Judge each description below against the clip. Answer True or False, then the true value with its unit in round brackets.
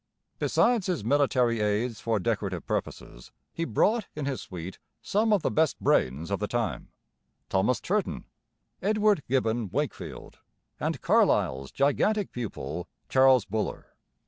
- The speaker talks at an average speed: False (130 wpm)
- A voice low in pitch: True (120 Hz)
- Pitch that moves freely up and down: True (8.3 semitones)